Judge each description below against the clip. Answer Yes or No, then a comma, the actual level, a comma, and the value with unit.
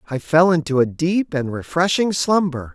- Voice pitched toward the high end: No, medium, 155 Hz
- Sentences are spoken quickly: No, average, 175 wpm